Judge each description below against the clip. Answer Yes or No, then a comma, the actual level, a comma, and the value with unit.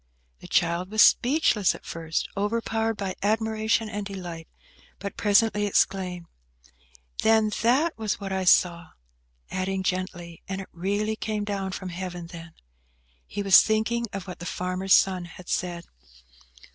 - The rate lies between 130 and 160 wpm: Yes, average, 145 wpm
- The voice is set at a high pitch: Yes, high, 195 Hz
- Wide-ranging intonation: No, average, 3.1 semitones